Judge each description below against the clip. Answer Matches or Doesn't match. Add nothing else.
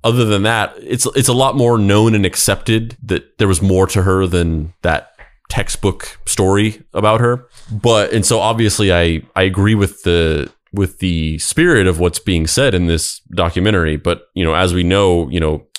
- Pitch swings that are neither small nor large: Matches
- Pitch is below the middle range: Matches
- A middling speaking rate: Matches